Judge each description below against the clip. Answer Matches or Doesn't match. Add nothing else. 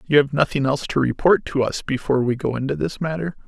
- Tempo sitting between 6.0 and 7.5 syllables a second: Matches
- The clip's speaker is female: Doesn't match